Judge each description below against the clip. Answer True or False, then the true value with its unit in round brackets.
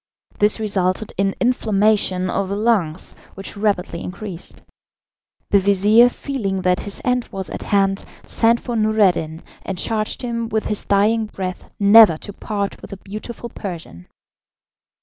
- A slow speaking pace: False (145 wpm)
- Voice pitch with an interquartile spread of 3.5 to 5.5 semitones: False (2.5 semitones)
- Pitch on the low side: False (200 Hz)